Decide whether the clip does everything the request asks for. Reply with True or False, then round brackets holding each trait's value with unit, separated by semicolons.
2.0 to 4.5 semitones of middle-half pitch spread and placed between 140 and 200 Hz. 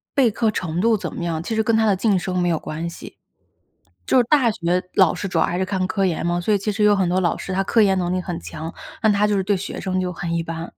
True (3.2 semitones; 185 Hz)